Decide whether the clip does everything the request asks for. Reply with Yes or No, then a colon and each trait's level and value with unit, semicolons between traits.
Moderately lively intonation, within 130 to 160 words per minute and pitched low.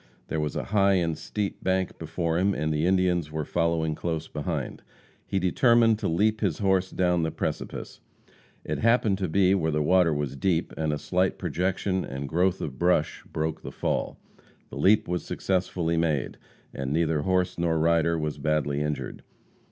No: average, 3.3 semitones; average, 175 wpm; very low, 85 Hz